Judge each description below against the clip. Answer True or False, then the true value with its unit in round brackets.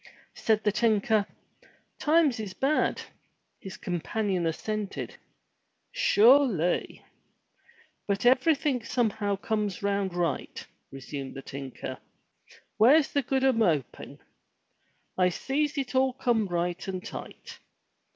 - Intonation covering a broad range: True (6.0 semitones)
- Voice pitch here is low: False (215 Hz)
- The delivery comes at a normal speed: False (110 wpm)